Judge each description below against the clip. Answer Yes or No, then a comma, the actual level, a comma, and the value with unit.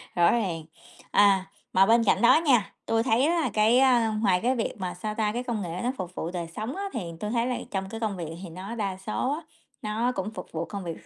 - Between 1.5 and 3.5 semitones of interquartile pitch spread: No, average, 4.2 semitones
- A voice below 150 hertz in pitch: No, high, 215 Hz